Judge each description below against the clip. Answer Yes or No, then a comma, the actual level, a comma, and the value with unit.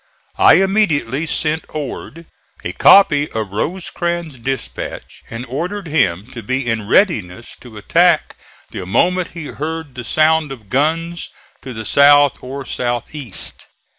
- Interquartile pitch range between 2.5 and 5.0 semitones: No, wide, 5.6 semitones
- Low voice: No, medium, 145 Hz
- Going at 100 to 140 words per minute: Yes, slow, 135 wpm